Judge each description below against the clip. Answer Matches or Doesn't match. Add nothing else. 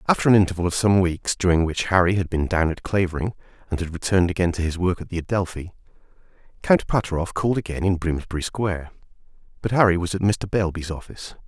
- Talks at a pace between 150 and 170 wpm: Doesn't match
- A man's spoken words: Matches